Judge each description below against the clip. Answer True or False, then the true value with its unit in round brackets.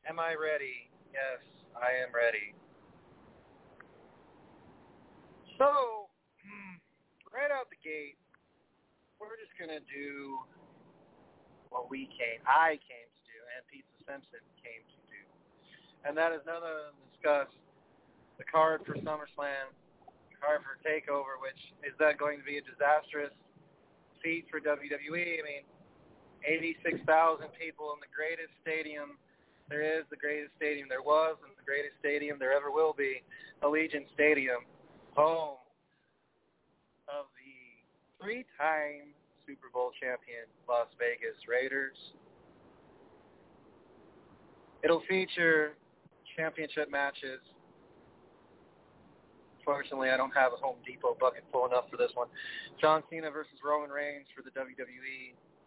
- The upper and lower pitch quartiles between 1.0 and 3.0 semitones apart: True (2.7 semitones)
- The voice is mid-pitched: True (150 Hz)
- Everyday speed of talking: False (125 wpm)